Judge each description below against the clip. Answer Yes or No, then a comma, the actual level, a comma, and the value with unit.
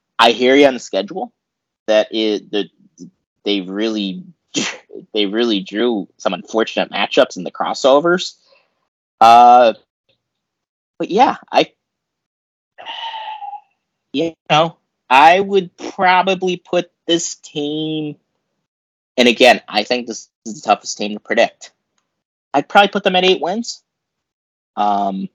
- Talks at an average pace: No, slow, 120 wpm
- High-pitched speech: No, medium, 145 Hz